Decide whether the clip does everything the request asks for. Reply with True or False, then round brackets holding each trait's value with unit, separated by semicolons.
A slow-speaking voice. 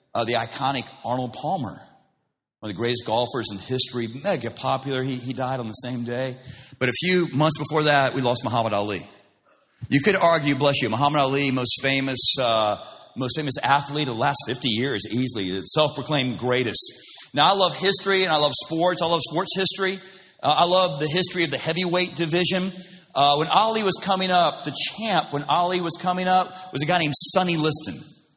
False (195 wpm)